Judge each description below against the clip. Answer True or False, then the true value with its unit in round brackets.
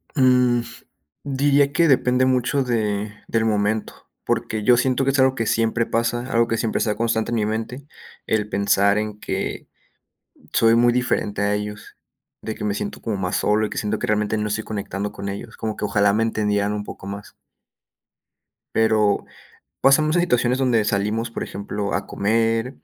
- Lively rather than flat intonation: False (3.0 semitones)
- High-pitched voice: False (110 Hz)